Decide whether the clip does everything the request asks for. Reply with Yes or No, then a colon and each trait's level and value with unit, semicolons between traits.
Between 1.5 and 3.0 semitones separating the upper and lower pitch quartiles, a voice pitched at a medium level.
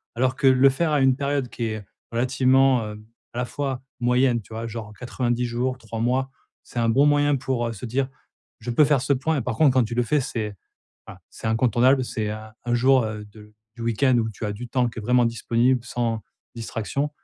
No: narrow, 2.5 semitones; low, 125 Hz